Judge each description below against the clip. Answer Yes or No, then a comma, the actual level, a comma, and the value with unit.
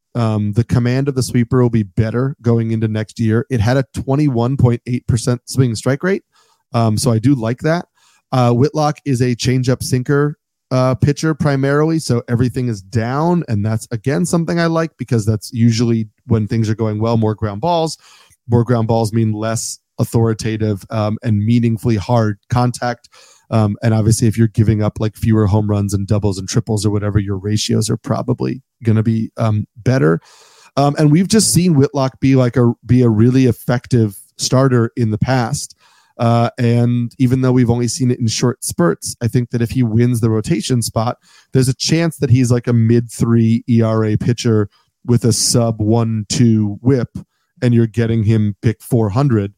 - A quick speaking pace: No, average, 185 wpm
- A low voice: Yes, low, 120 Hz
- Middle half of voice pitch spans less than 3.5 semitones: Yes, narrow, 2.6 semitones